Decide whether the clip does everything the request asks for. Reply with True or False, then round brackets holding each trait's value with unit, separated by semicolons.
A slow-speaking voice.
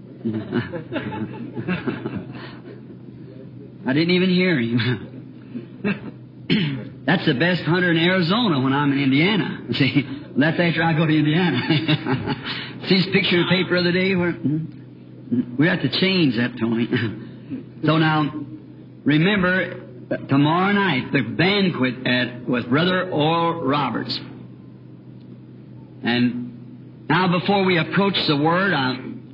True (120 wpm)